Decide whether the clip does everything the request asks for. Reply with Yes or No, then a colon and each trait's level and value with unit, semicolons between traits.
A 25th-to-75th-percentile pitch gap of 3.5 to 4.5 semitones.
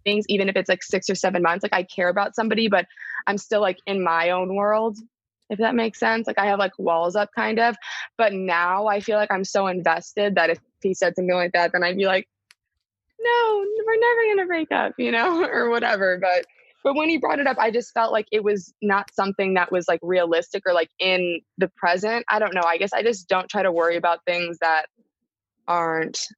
Yes: average, 3.9 semitones